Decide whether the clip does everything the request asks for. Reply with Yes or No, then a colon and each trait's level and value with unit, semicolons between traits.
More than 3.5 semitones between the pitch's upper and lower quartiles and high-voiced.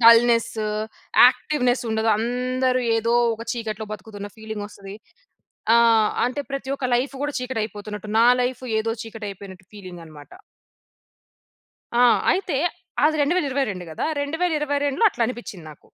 Yes: average, 4.1 semitones; high, 230 Hz